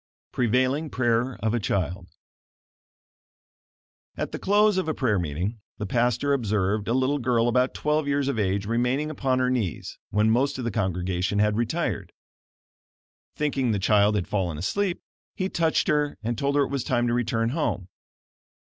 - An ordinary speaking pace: Yes, average, 165 wpm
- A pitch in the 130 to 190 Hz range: No, low, 120 Hz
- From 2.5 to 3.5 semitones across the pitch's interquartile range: No, average, 5.1 semitones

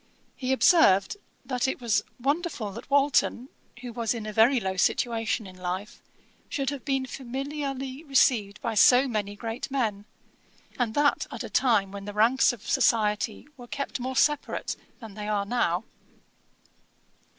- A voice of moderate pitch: No, high, 240 Hz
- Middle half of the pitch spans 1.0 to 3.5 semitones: No, average, 4.3 semitones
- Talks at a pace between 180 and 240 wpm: No, average, 155 wpm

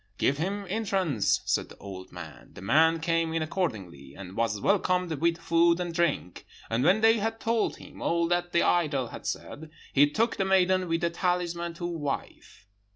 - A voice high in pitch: No, medium, 170 Hz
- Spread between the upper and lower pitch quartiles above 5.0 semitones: No, average, 4.2 semitones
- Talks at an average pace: Yes, average, 185 wpm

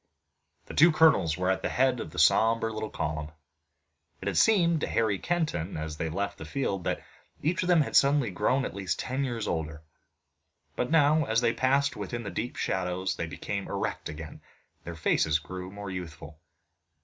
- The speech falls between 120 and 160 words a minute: No, average, 190 wpm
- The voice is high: No, low, 100 Hz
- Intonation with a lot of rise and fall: Yes, wide, 8.2 semitones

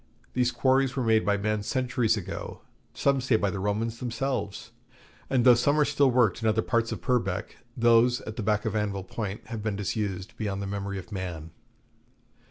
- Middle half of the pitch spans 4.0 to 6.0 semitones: No, average, 3.5 semitones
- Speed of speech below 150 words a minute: No, average, 190 wpm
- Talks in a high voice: No, low, 110 Hz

